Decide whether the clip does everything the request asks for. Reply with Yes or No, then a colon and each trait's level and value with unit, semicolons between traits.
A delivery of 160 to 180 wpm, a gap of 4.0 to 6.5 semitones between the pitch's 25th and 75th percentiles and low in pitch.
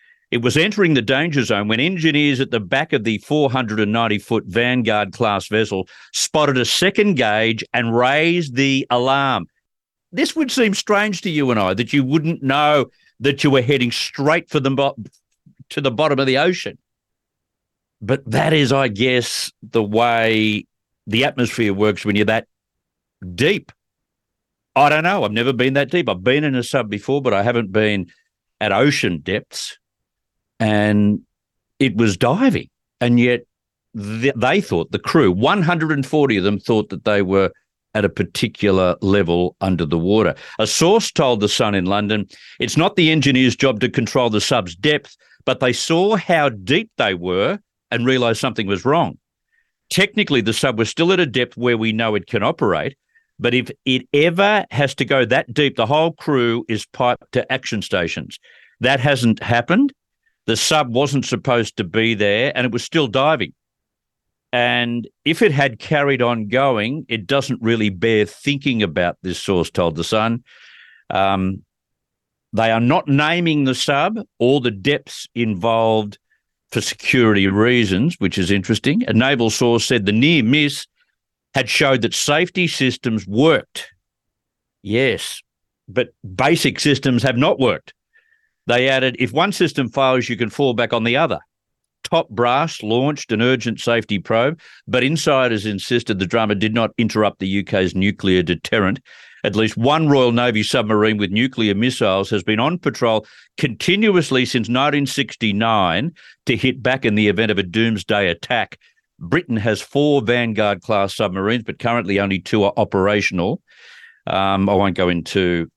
Yes: average, 165 wpm; average, 4.8 semitones; low, 120 Hz